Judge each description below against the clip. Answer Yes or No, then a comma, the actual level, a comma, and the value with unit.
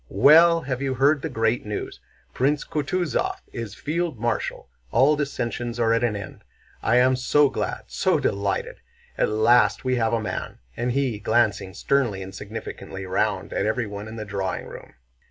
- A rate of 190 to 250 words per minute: No, average, 170 wpm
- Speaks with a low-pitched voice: Yes, low, 120 Hz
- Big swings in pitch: No, average, 4.6 semitones